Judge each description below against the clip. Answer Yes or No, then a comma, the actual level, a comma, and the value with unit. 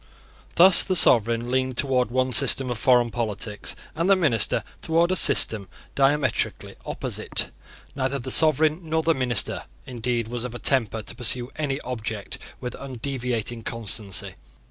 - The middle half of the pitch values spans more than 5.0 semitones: No, average, 3.2 semitones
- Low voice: Yes, low, 125 Hz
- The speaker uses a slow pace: No, average, 145 wpm